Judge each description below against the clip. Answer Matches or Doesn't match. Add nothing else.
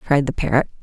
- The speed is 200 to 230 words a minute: Matches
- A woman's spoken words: Matches